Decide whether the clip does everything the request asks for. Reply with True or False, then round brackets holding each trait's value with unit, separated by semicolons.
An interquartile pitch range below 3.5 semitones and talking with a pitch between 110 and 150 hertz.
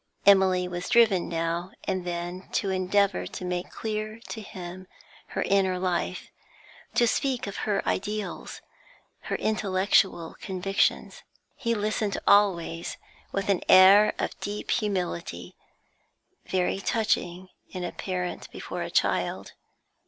False (2.5 semitones; 190 Hz)